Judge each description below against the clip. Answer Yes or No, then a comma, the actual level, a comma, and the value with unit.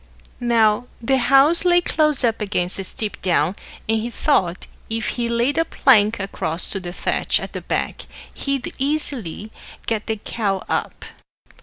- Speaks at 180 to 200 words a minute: No, average, 160 wpm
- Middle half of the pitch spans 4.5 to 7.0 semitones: Yes, average, 5.0 semitones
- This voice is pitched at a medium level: No, high, 225 Hz